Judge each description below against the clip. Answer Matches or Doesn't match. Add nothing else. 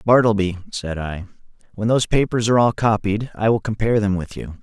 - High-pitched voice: Doesn't match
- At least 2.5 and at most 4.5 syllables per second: Doesn't match